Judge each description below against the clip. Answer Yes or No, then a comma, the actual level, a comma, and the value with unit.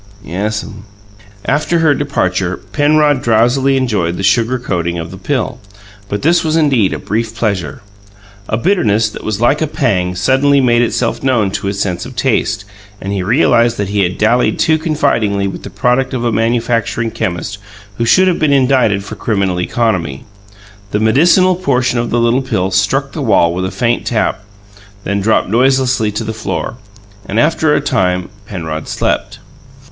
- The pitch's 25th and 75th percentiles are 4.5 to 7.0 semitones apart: Yes, average, 5.2 semitones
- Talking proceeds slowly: No, average, 170 wpm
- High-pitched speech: No, low, 115 Hz